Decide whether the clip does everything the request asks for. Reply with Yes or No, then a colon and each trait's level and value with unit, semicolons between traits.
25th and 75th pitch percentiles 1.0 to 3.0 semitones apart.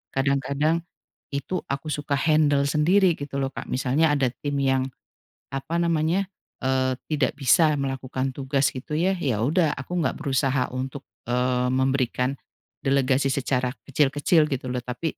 Yes: narrow, 2.6 semitones